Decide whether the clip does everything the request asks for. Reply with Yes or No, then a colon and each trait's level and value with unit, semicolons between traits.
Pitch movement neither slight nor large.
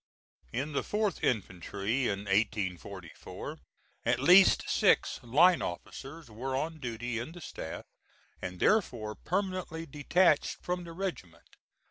No: wide, 8.3 semitones